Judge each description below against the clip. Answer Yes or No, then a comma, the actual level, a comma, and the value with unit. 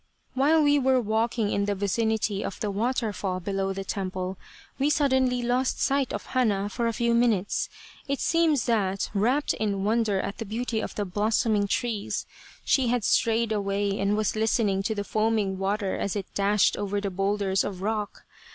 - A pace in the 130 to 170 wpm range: No, average, 185 wpm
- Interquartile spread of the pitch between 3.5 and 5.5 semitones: No, average, 3.1 semitones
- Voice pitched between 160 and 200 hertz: No, high, 215 Hz